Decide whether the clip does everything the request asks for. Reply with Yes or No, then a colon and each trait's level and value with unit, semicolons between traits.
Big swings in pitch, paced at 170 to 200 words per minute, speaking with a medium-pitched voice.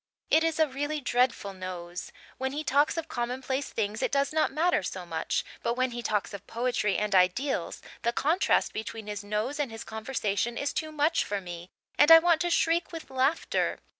No: wide, 6.3 semitones; average, 195 wpm; very high, 255 Hz